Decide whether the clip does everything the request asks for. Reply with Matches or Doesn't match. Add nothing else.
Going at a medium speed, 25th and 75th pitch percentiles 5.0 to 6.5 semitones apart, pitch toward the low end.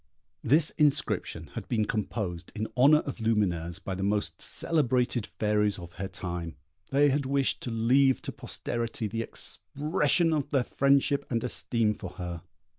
Matches